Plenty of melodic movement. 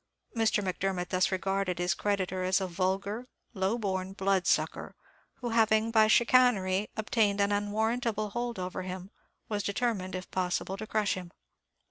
No: average, 2.7 semitones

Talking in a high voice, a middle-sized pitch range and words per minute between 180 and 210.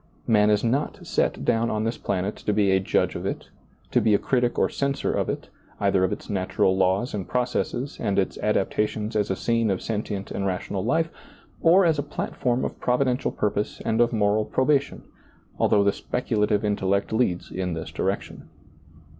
No: low, 105 Hz; average, 3.7 semitones; average, 185 wpm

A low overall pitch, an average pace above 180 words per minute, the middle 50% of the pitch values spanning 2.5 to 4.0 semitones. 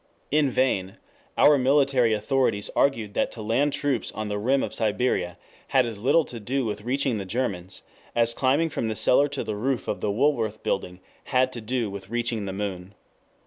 No: low, 115 Hz; average, 190 wpm; average, 4.5 semitones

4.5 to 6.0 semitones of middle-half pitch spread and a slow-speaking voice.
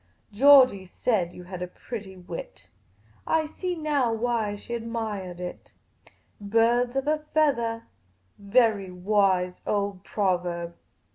Yes: average, 4.8 semitones; slow, 120 wpm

